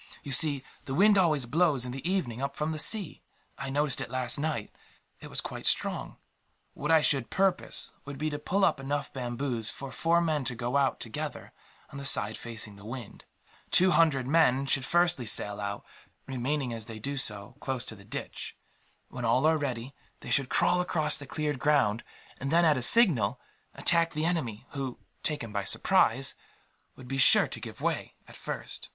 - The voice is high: No, low, 135 Hz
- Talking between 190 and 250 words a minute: Yes, average, 195 wpm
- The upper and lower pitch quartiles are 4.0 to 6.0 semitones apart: Yes, average, 4.3 semitones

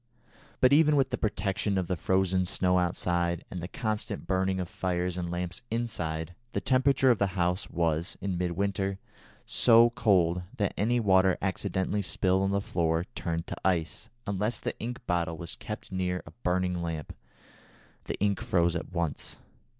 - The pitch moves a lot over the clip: No, average, 2.8 semitones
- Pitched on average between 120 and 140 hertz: No, very low, 95 Hz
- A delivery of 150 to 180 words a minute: Yes, average, 170 wpm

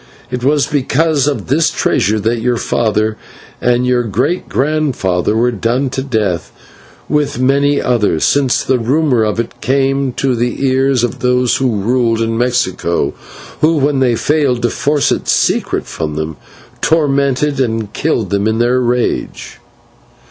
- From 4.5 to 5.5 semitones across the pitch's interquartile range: No, average, 3.5 semitones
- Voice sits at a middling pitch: No, low, 125 Hz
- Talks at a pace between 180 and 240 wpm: No, average, 155 wpm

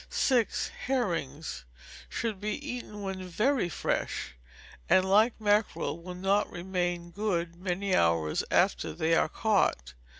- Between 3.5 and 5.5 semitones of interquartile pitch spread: Yes, average, 3.8 semitones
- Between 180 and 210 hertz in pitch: Yes, medium, 185 Hz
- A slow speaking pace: Yes, slow, 125 wpm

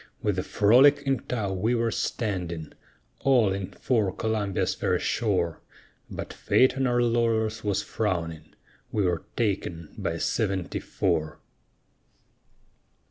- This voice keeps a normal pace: No, slow, 130 wpm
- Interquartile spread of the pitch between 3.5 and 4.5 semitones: Yes, average, 4.2 semitones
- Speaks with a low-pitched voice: Yes, low, 105 Hz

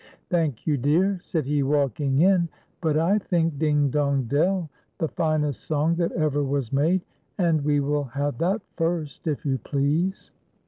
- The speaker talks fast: No, average, 175 wpm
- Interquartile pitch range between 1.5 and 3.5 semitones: Yes, average, 3.0 semitones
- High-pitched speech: No, medium, 150 Hz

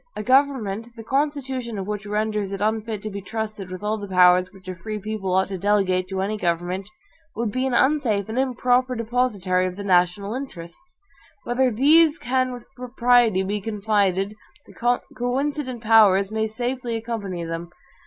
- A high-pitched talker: Yes, high, 215 Hz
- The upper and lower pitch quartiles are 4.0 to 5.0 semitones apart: Yes, average, 4.3 semitones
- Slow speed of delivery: No, average, 170 wpm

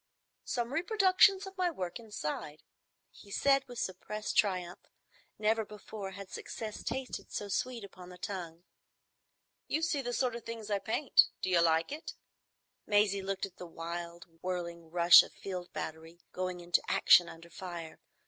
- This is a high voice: Yes, high, 195 Hz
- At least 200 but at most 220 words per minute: No, average, 160 wpm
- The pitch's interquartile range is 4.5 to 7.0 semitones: Yes, average, 5.1 semitones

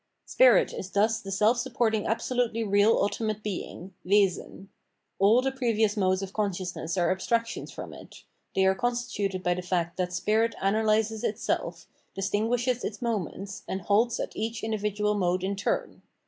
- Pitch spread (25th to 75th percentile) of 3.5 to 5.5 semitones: No, average, 2.8 semitones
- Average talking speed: Yes, average, 155 wpm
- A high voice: Yes, high, 210 Hz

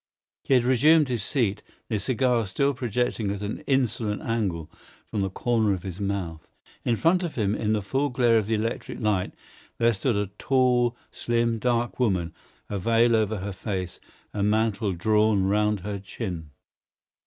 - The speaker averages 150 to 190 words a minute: Yes, average, 170 wpm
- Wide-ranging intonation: No, average, 3.3 semitones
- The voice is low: Yes, low, 110 Hz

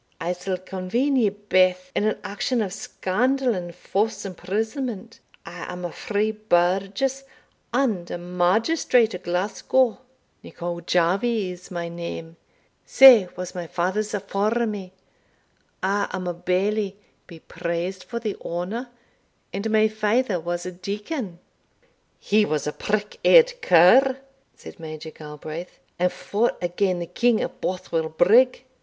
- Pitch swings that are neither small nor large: Yes, average, 3.9 semitones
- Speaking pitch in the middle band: No, high, 195 Hz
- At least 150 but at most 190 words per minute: No, slow, 135 wpm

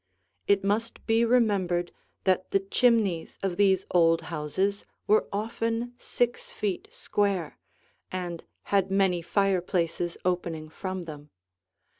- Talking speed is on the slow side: Yes, slow, 115 wpm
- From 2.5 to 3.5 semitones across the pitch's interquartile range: Yes, average, 3.1 semitones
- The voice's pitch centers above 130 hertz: Yes, high, 190 Hz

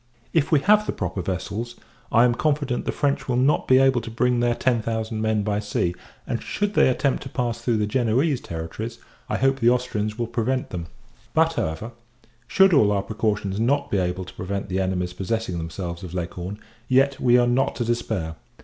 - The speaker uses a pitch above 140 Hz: No, low, 115 Hz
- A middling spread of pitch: Yes, average, 4.8 semitones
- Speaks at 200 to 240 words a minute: Yes, fast, 205 wpm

